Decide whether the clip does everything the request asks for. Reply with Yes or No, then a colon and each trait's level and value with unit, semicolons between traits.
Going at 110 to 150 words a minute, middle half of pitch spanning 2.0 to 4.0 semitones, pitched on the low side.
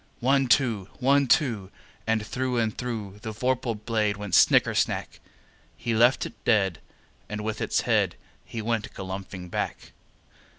Yes: average, 145 wpm; average, 3.0 semitones; low, 110 Hz